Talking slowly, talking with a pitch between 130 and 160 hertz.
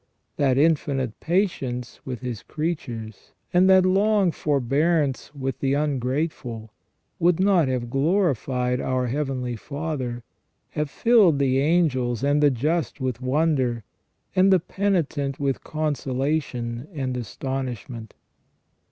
Yes: slow, 115 wpm; medium, 140 Hz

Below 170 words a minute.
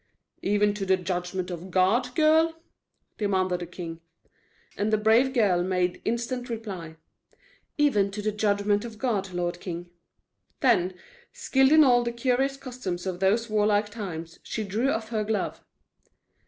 Yes: average, 150 wpm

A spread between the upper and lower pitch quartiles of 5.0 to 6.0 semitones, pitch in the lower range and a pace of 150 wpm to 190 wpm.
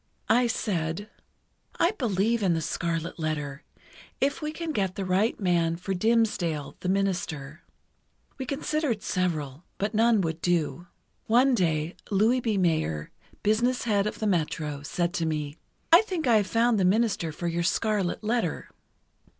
No: wide, 5.5 semitones; high, 190 Hz; average, 155 wpm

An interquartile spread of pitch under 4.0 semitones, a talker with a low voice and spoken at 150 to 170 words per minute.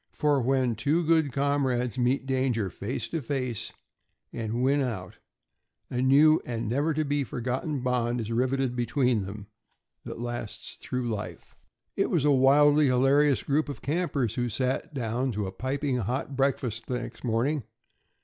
Yes: average, 3.0 semitones; low, 130 Hz; average, 160 wpm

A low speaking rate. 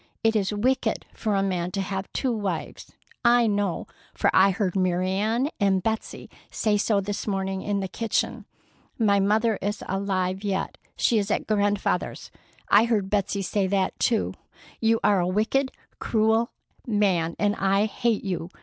No: average, 165 wpm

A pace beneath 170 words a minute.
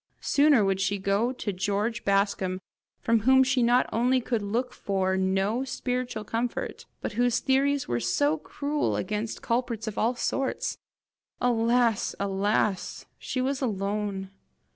Yes: average, 140 wpm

